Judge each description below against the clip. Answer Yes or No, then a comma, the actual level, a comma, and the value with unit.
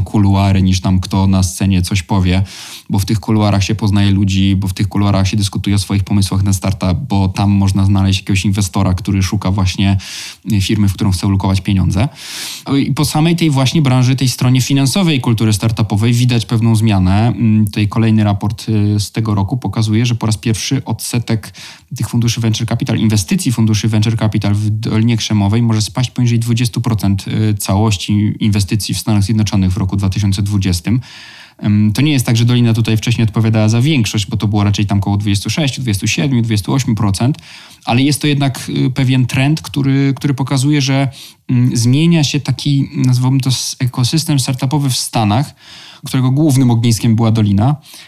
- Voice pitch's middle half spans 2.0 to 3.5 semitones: No, average, 4.0 semitones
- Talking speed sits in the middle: No, fast, 165 wpm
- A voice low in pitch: Yes, low, 110 Hz